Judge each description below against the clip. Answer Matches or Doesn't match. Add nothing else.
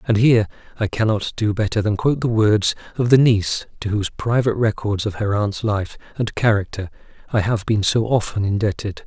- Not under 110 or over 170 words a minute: Doesn't match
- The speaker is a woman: Doesn't match